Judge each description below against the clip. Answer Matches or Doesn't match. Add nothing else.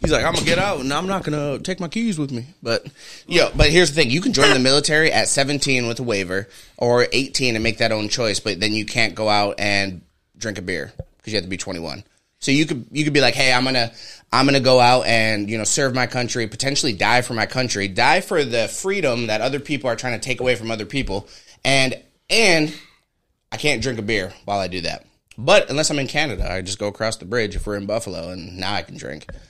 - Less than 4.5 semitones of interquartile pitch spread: Doesn't match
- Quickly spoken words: Matches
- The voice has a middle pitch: Doesn't match